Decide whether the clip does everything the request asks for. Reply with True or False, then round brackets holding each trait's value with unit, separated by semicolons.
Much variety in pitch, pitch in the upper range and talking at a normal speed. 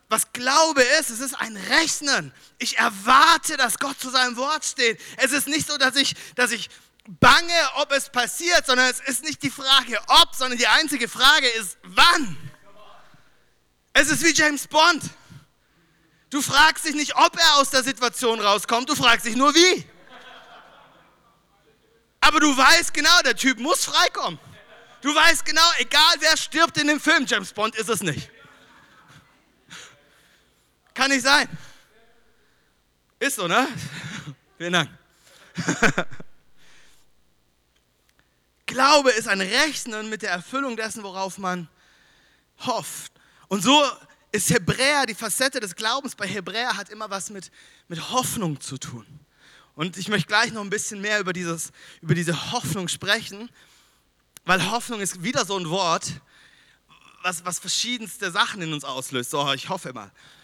True (7.6 semitones; 235 Hz; 150 wpm)